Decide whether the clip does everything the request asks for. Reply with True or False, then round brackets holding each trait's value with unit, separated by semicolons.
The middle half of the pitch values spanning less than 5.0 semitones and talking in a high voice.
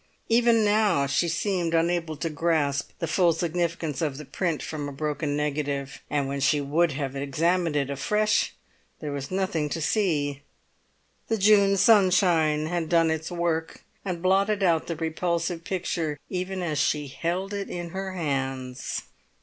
False (3.9 semitones; 165 Hz)